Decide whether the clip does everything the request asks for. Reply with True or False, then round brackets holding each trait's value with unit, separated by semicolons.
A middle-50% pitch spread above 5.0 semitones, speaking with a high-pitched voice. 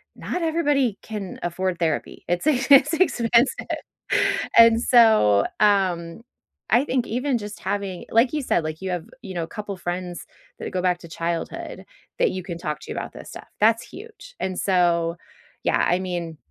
True (5.6 semitones; 195 Hz)